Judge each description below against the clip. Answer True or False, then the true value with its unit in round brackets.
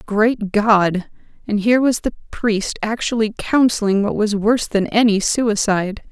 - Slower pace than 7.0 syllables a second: True (4.5 syllables/s)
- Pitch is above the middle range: True (215 Hz)